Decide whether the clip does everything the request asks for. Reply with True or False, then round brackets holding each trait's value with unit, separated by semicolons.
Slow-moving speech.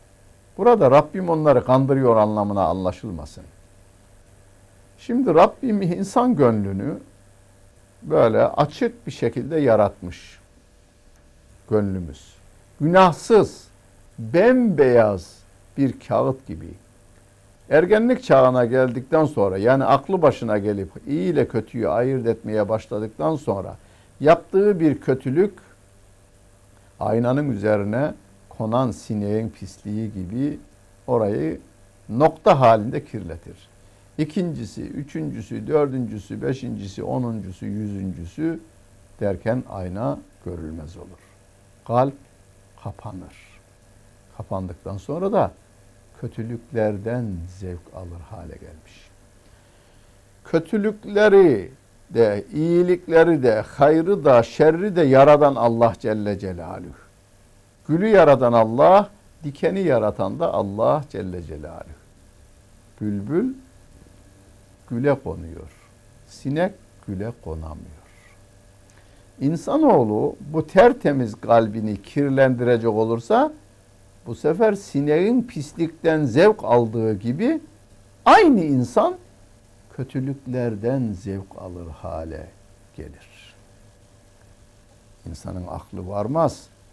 True (80 wpm)